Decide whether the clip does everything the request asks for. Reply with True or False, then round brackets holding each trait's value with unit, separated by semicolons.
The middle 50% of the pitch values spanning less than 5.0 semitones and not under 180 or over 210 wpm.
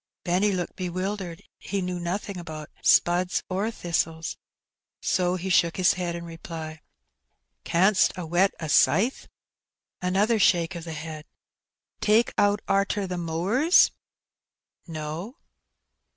False (2.9 semitones; 150 wpm)